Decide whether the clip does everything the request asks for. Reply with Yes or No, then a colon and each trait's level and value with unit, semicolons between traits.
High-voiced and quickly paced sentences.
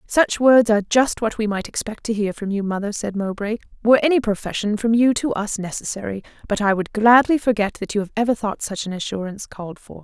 Yes: high, 215 Hz; fast, 225 wpm